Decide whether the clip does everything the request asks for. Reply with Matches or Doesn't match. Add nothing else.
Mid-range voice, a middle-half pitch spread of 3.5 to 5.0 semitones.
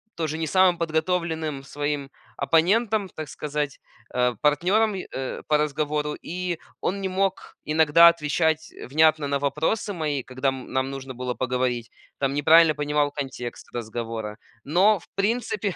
Matches